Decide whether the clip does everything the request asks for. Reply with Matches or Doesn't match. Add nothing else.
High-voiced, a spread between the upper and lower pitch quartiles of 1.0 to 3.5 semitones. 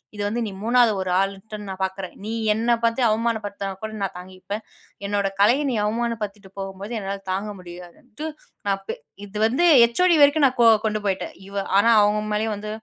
Matches